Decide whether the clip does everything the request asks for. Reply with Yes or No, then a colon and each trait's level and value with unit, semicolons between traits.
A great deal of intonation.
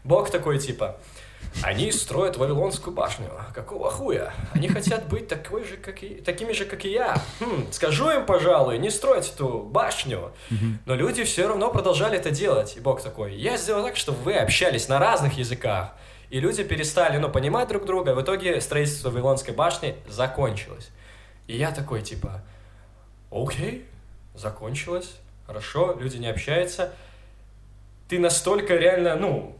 Yes: wide, 8.6 semitones